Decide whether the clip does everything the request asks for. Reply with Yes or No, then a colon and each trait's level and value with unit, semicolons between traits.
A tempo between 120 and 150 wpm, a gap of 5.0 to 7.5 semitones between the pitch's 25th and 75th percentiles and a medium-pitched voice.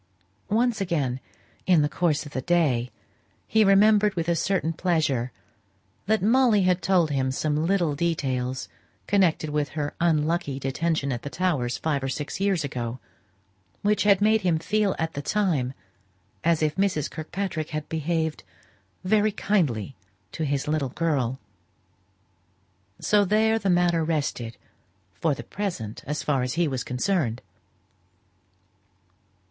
Yes: average, 140 wpm; wide, 5.5 semitones; medium, 160 Hz